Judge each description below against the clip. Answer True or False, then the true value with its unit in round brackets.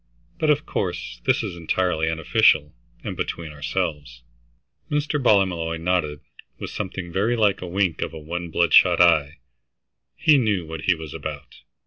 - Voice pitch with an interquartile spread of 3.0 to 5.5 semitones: True (3.6 semitones)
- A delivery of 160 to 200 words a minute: False (145 wpm)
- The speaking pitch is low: True (85 Hz)